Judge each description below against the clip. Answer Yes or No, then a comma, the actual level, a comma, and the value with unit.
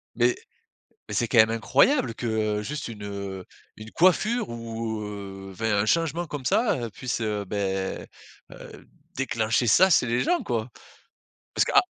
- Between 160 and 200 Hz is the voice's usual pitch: No, low, 115 Hz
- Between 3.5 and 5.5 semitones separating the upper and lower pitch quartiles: Yes, average, 3.9 semitones